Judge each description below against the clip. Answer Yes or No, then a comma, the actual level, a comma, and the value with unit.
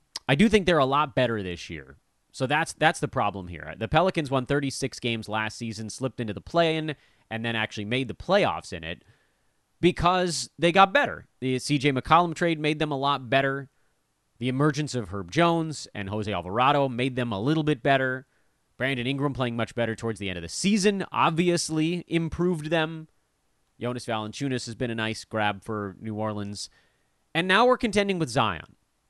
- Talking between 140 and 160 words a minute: No, average, 190 wpm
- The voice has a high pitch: No, low, 130 Hz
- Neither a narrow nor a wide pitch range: No, wide, 6.2 semitones